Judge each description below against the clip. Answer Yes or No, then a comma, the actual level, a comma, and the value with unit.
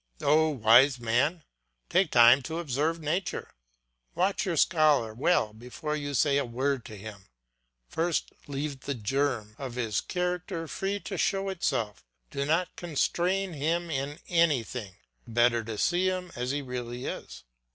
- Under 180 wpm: Yes, average, 150 wpm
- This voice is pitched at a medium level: Yes, medium, 145 Hz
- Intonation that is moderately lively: No, wide, 5.7 semitones